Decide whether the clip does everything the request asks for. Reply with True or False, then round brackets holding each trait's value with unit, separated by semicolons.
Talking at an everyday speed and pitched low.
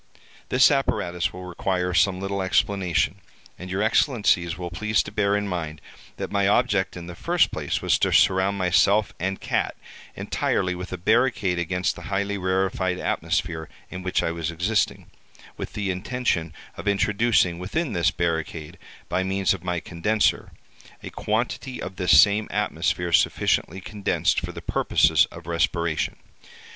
True (155 wpm; 95 Hz)